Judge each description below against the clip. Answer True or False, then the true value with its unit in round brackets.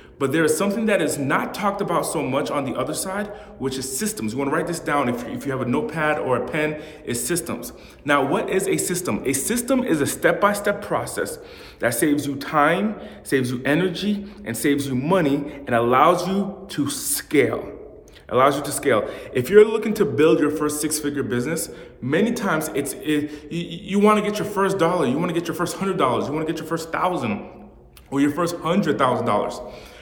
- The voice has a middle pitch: True (165 Hz)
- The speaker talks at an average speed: False (215 wpm)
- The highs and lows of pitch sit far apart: True (5.7 semitones)